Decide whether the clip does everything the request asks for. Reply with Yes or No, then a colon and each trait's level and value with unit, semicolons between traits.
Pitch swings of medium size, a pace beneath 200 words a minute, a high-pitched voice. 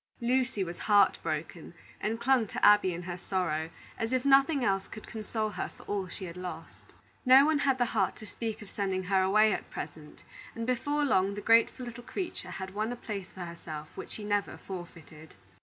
No: average, 4.5 semitones; fast, 205 wpm; high, 210 Hz